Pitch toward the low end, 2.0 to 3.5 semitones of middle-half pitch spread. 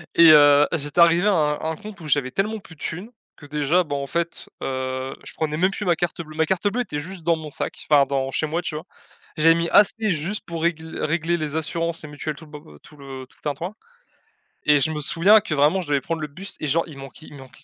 No: medium, 160 Hz; average, 2.8 semitones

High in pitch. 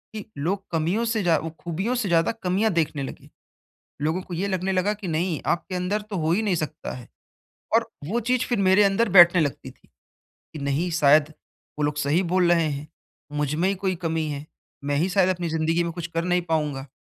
No: medium, 170 Hz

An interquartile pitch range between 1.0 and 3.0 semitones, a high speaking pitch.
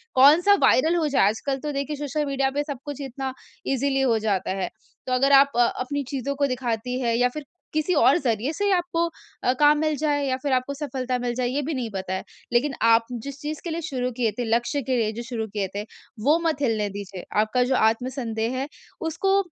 No: average, 3.6 semitones; very high, 265 Hz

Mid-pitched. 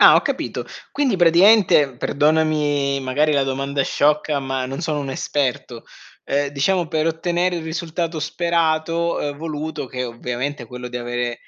Yes: medium, 150 Hz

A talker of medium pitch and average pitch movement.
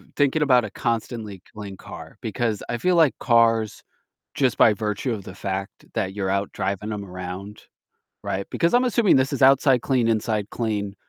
No: low, 110 Hz; average, 4.6 semitones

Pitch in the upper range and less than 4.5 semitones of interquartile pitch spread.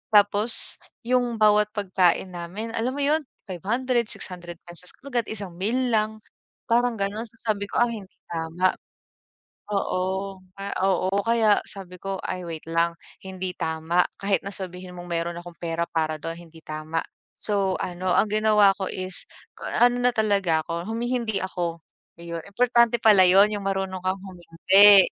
Yes: high, 195 Hz; average, 3.8 semitones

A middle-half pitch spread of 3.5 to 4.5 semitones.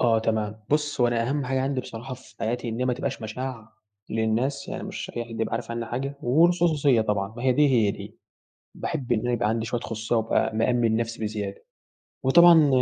No: average, 3.0 semitones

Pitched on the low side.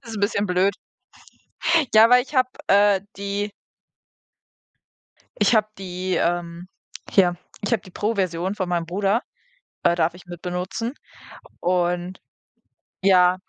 No: medium, 185 Hz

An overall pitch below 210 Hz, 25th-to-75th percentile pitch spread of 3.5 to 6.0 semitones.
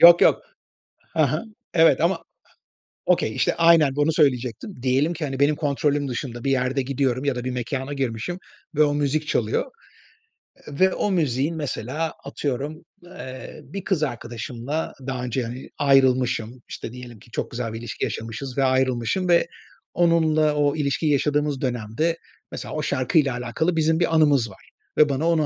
Yes: medium, 140 Hz; average, 3.8 semitones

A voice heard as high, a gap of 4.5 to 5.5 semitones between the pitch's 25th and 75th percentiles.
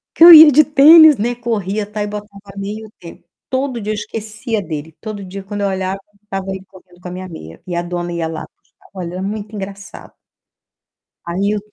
No: high, 200 Hz; average, 2.7 semitones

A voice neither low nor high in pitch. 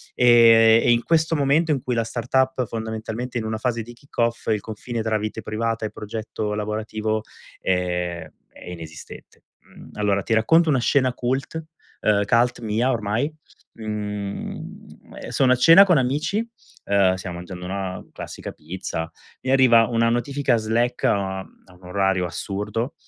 No: low, 115 Hz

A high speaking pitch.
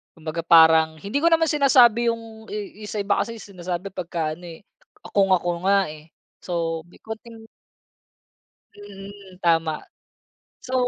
Yes: high, 195 Hz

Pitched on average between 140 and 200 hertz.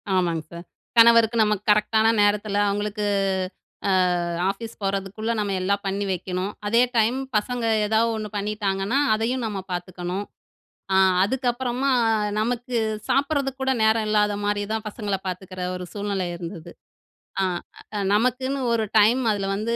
No: high, 210 Hz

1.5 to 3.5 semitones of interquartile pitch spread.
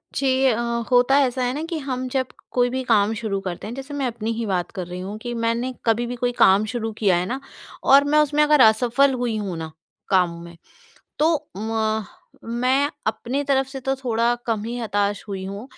No: average, 4.1 semitones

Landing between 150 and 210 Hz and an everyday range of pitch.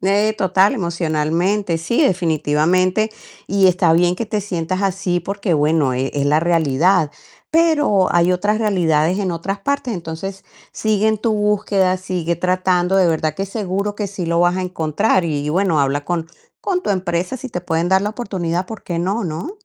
Yes: medium, 185 Hz; average, 3.4 semitones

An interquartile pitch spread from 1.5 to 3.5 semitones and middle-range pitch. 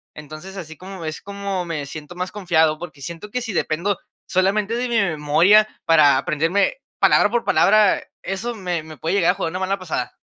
No: average, 4.1 semitones; medium, 180 Hz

